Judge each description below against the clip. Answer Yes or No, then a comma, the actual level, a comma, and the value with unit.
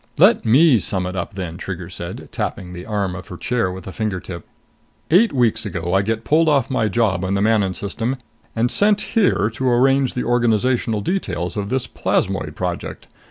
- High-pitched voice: No, low, 110 Hz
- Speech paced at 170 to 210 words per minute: Yes, average, 195 wpm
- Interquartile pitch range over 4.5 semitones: Yes, average, 5.1 semitones